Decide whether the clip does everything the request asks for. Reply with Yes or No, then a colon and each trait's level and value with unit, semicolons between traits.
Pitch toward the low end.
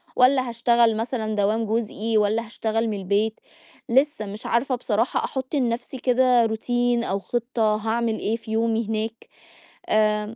No: high, 225 Hz